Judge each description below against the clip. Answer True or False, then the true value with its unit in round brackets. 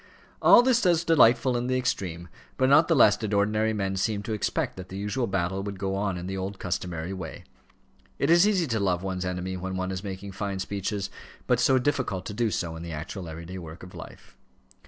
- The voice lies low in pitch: True (100 Hz)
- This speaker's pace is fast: True (220 wpm)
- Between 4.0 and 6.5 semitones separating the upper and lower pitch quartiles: True (4.3 semitones)